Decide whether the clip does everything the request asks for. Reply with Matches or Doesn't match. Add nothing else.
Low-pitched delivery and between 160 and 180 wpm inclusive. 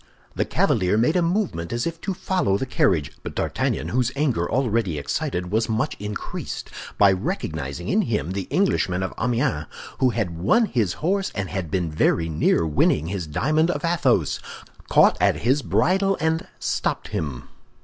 Matches